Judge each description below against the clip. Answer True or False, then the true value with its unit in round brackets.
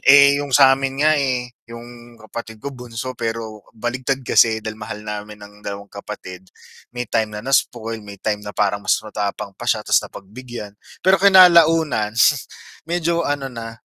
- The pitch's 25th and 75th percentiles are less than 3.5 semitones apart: False (4.2 semitones)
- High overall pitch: False (115 Hz)